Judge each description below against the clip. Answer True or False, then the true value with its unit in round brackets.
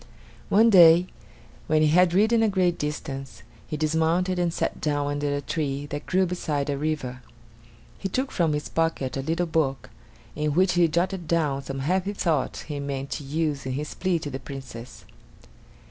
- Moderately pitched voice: True (155 Hz)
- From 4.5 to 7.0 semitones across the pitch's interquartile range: False (3.8 semitones)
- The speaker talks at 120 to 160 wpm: False (185 wpm)